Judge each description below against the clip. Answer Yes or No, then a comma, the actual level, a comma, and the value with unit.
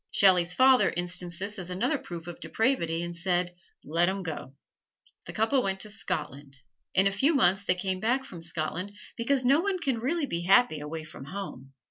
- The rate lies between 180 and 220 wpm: Yes, average, 190 wpm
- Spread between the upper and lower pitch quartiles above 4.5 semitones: Yes, average, 5.3 semitones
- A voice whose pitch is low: No, medium, 185 Hz